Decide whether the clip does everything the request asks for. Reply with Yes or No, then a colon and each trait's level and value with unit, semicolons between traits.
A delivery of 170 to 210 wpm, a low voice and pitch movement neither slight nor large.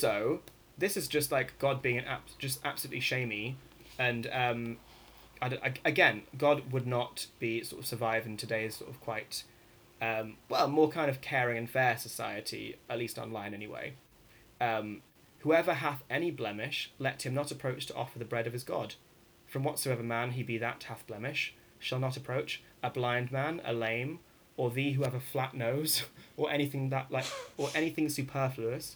Yes: average, 180 wpm; low, 130 Hz; average, 3.5 semitones